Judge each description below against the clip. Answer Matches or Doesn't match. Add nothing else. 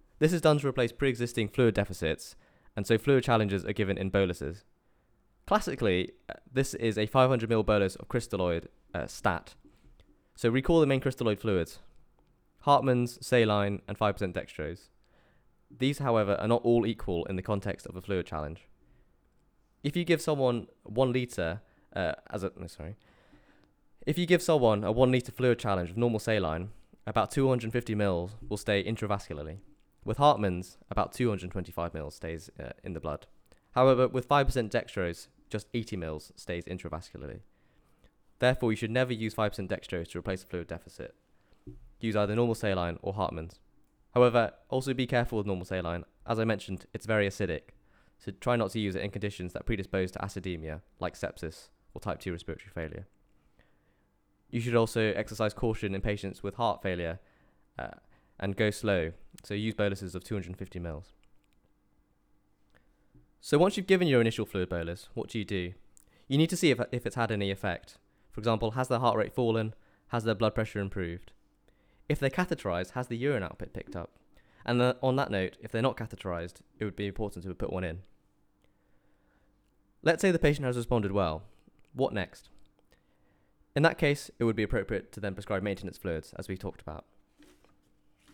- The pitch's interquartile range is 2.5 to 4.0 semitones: Doesn't match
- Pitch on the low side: Matches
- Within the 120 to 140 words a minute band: Doesn't match